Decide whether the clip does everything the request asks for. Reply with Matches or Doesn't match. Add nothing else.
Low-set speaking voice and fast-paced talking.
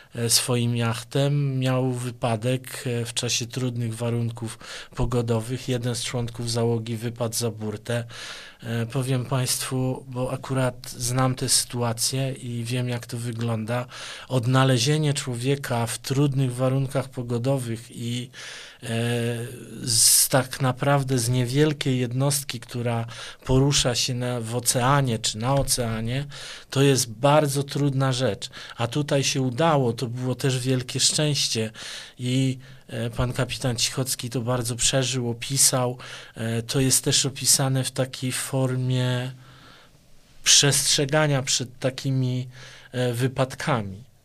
Doesn't match